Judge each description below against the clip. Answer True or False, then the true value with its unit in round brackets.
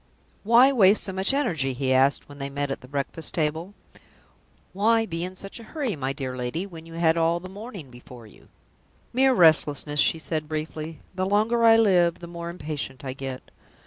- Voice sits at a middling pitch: True (165 Hz)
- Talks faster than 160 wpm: True (195 wpm)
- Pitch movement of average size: False (5.7 semitones)